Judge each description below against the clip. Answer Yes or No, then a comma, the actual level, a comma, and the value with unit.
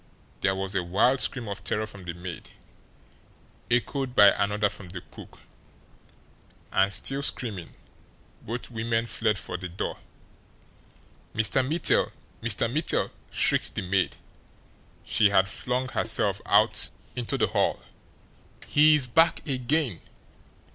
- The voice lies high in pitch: No, low, 110 Hz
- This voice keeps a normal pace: No, slow, 125 wpm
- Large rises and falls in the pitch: No, average, 4.8 semitones